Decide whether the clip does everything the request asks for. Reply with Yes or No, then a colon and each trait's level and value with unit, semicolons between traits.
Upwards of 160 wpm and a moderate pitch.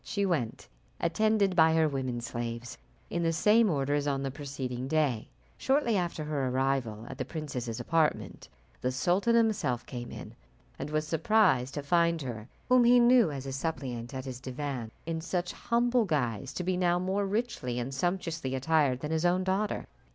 Yes: average, 180 wpm; medium, 155 Hz